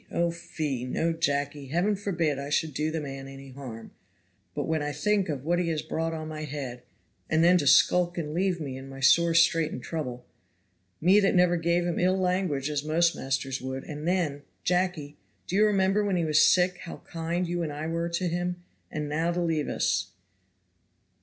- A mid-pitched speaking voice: Yes, medium, 165 Hz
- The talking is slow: No, fast, 205 wpm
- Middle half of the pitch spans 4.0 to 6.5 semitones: No, average, 3.3 semitones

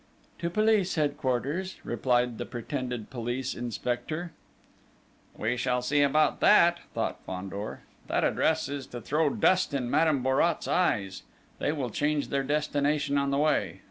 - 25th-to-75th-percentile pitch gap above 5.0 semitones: No, average, 4.0 semitones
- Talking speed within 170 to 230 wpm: No, average, 140 wpm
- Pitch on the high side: No, medium, 140 Hz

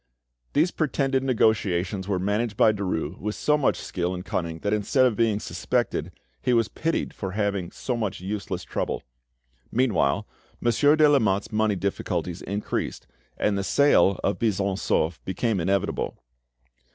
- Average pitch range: Yes, average, 3.9 semitones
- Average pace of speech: Yes, average, 150 wpm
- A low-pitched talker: Yes, low, 105 Hz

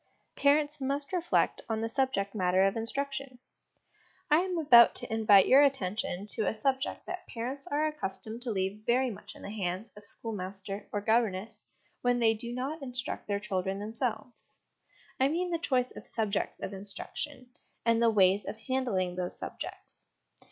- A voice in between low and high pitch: No, high, 230 Hz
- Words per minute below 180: Yes, average, 165 wpm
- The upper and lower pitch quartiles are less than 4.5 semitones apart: No, average, 5.0 semitones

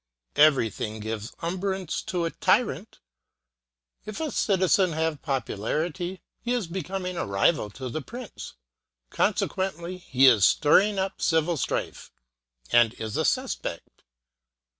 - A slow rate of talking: Yes, slow, 125 wpm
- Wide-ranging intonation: Yes, wide, 6.8 semitones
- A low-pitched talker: No, medium, 165 Hz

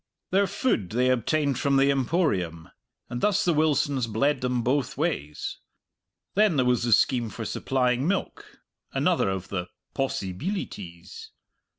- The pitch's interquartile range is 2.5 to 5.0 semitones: No, wide, 5.5 semitones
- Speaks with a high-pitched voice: No, low, 130 Hz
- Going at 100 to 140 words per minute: Yes, slow, 135 wpm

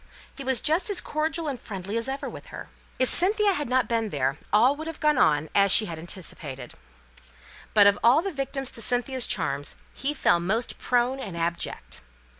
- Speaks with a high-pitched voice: Yes, high, 240 Hz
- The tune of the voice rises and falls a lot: Yes, wide, 8.1 semitones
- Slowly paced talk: No, average, 195 wpm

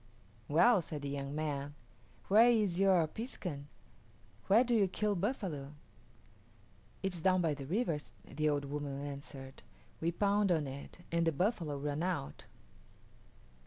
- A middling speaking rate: Yes, average, 145 wpm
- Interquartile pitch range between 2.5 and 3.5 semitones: No, average, 5.3 semitones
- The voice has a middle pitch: Yes, medium, 165 Hz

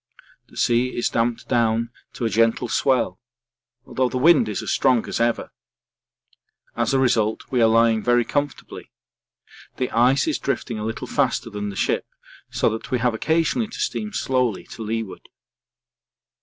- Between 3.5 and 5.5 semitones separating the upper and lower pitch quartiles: No, narrow, 2.5 semitones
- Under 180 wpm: Yes, average, 165 wpm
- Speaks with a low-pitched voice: Yes, low, 120 Hz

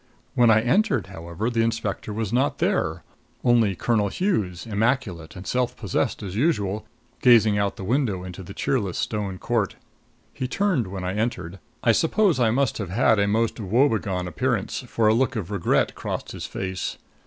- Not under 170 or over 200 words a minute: Yes, average, 175 wpm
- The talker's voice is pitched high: No, low, 110 Hz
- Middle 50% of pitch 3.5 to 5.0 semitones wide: Yes, average, 4.0 semitones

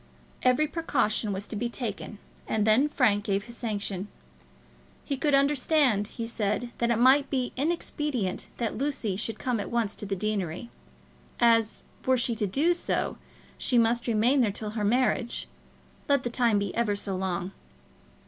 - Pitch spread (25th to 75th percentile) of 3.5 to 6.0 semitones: Yes, average, 3.8 semitones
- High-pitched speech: Yes, high, 235 Hz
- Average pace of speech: Yes, average, 165 wpm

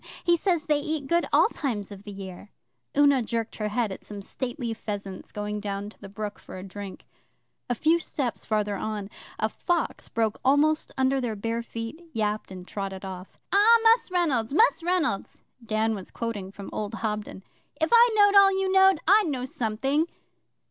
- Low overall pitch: No, high, 230 Hz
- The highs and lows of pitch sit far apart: Yes, wide, 7.1 semitones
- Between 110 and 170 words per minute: No, average, 185 wpm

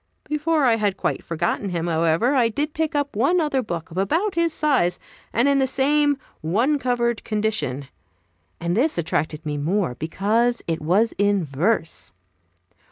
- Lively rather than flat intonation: Yes, wide, 8.8 semitones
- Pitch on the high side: Yes, high, 220 Hz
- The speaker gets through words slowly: No, average, 165 wpm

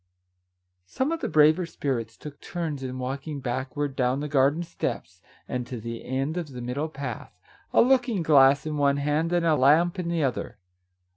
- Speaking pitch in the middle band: Yes, medium, 145 Hz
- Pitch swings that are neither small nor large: Yes, average, 3.7 semitones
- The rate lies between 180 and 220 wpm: Yes, average, 185 wpm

